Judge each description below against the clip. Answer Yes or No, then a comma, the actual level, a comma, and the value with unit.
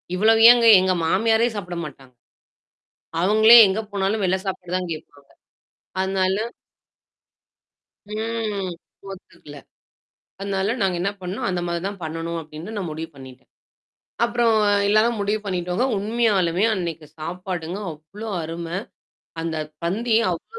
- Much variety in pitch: No, average, 4.1 semitones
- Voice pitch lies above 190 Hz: No, medium, 185 Hz